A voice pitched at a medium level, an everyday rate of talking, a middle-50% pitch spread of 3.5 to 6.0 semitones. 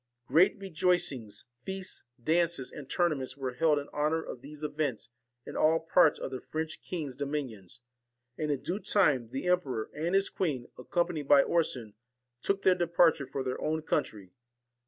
Yes: medium, 150 Hz; average, 160 wpm; average, 4.6 semitones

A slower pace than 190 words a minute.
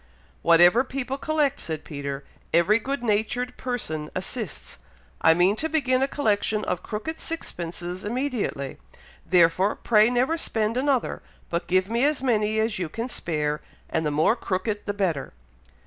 Yes: average, 150 wpm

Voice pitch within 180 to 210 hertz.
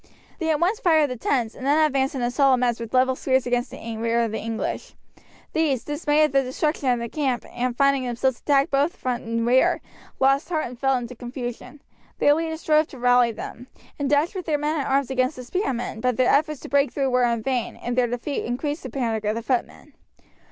No: very high, 260 Hz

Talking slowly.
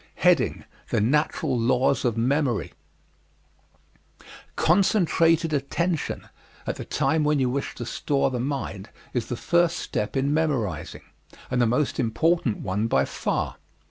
Yes: slow, 130 wpm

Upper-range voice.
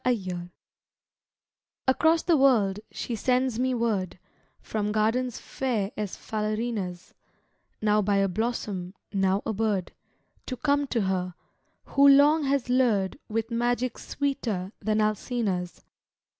Yes: high, 220 Hz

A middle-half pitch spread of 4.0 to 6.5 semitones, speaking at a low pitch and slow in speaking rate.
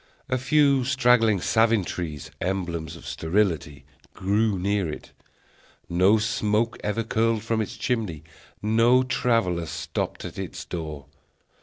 Yes: average, 4.9 semitones; low, 105 Hz; slow, 125 wpm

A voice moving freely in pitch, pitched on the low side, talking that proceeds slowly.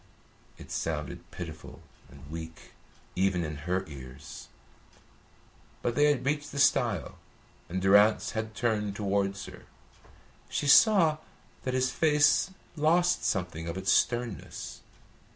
Yes: wide, 7.6 semitones; low, 105 Hz; slow, 120 wpm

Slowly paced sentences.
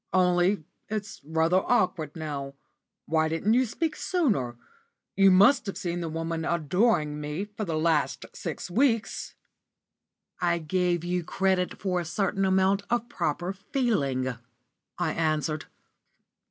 Yes: slow, 130 wpm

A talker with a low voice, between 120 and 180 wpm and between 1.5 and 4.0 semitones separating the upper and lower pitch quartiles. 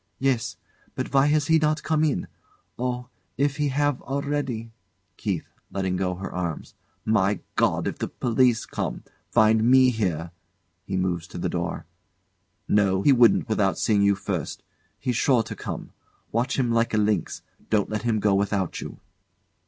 No: low, 110 Hz; average, 165 wpm; average, 5.0 semitones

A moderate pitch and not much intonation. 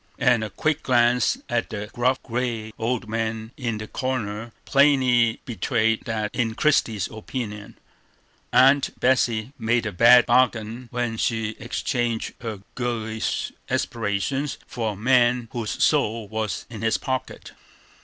No: low, 115 Hz; narrow, 2.2 semitones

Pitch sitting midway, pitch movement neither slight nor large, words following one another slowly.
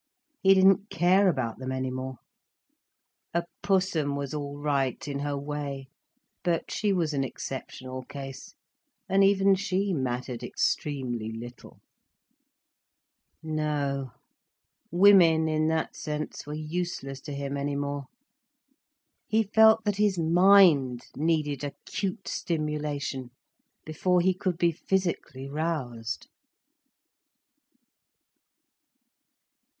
Yes: medium, 150 Hz; average, 4.8 semitones; slow, 105 wpm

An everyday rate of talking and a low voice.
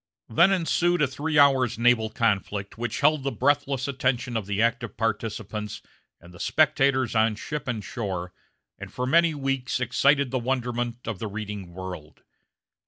Yes: average, 160 wpm; low, 120 Hz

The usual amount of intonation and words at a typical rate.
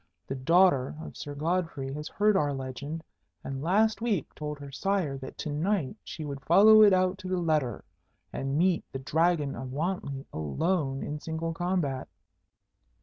Yes: average, 5.0 semitones; average, 165 wpm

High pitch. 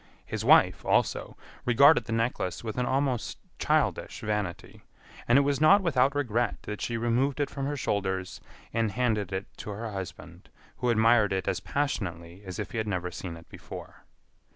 No: low, 115 Hz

